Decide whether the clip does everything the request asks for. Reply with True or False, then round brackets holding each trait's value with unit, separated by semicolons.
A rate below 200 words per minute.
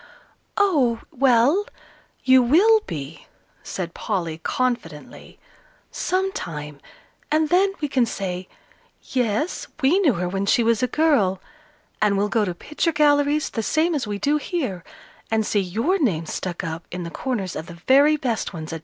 True (160 wpm)